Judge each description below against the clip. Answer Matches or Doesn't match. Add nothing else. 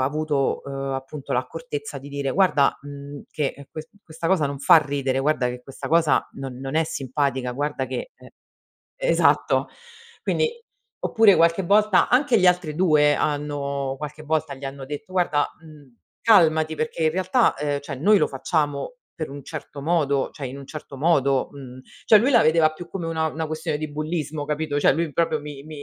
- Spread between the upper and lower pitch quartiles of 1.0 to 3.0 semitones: Matches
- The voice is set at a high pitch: Doesn't match